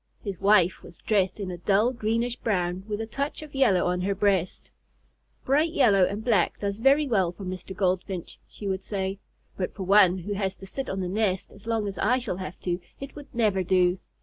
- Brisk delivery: Yes, fast, 215 wpm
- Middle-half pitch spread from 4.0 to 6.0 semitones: No, average, 3.3 semitones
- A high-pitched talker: Yes, high, 200 Hz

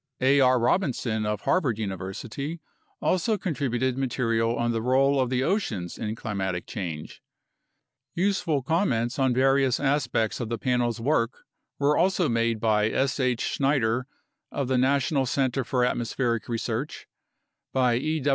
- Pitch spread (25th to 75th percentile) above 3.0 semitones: Yes, average, 3.4 semitones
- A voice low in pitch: Yes, low, 125 Hz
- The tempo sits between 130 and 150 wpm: Yes, average, 140 wpm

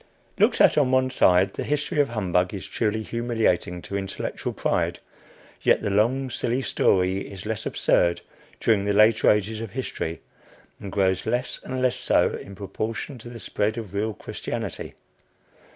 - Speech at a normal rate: Yes, average, 165 wpm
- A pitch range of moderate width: Yes, average, 3.7 semitones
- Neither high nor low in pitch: No, low, 110 Hz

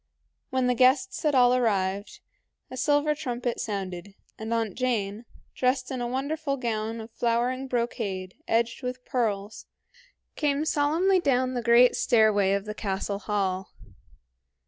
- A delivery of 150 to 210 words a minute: No, average, 140 wpm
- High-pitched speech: Yes, high, 240 Hz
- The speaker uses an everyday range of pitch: Yes, average, 3.6 semitones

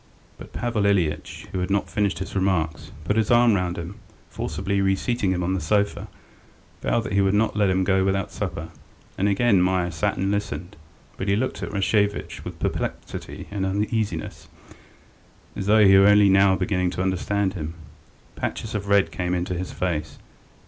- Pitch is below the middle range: Yes, very low, 95 Hz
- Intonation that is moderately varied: No, narrow, 2.0 semitones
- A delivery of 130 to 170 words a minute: No, average, 185 wpm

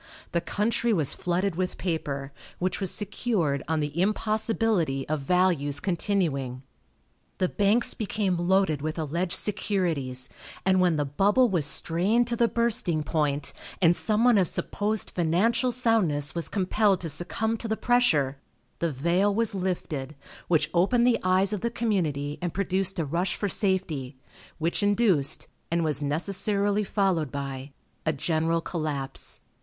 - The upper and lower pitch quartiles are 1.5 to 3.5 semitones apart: No, average, 5.1 semitones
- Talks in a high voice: No, medium, 180 Hz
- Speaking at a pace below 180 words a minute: Yes, average, 150 wpm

